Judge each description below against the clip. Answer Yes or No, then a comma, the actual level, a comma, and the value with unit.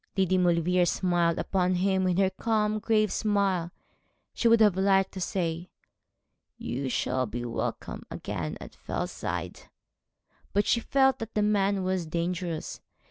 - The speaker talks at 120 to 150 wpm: Yes, average, 140 wpm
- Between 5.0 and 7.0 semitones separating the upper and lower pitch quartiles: No, average, 3.1 semitones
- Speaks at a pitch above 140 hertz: Yes, medium, 185 Hz